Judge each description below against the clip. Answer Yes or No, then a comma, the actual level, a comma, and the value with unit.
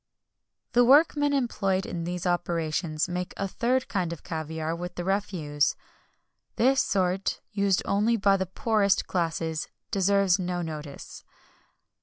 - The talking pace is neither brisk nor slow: No, slow, 130 wpm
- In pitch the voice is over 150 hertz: Yes, medium, 185 Hz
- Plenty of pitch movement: No, average, 3.2 semitones